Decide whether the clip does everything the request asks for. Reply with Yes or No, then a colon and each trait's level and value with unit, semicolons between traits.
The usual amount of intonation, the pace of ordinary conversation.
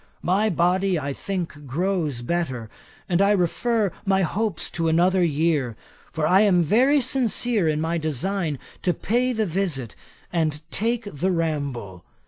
Yes: average, 4.5 semitones; average, 145 wpm